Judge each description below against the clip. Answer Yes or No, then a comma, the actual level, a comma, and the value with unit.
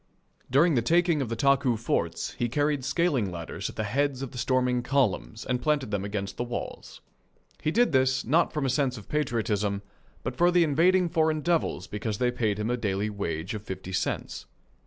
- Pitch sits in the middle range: No, low, 125 Hz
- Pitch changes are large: Yes, wide, 5.8 semitones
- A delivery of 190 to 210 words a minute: Yes, average, 200 wpm